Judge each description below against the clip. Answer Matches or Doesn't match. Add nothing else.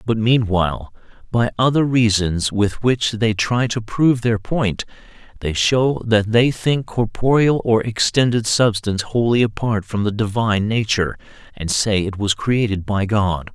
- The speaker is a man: Matches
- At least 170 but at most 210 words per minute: Doesn't match